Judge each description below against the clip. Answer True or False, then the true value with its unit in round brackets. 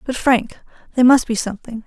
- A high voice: True (235 Hz)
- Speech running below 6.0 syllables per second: False (6.2 syllables/s)